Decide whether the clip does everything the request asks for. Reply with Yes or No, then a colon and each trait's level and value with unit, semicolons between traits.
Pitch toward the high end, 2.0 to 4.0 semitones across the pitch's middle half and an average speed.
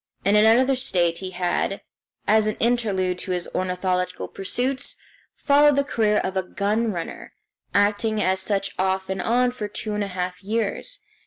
Yes: high, 205 Hz; average, 3.5 semitones; average, 165 wpm